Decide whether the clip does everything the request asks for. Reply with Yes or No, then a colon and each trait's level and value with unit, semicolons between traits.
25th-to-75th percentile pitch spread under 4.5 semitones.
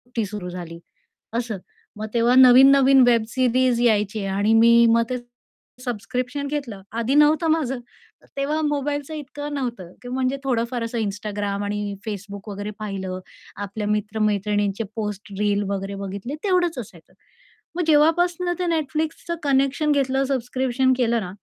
No: average, 5.0 semitones